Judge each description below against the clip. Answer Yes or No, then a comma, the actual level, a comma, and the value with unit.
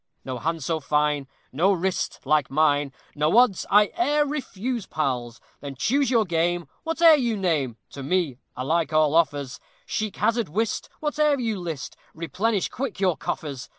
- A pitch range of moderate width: No, wide, 7.6 semitones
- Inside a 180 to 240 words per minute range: No, average, 155 wpm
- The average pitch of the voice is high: No, medium, 170 Hz